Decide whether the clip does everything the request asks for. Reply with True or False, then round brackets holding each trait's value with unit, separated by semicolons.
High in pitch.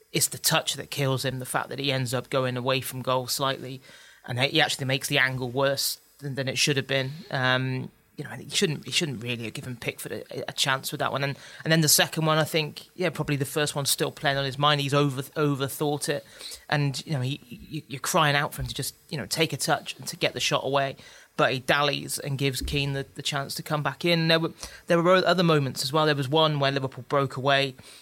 False (140 Hz)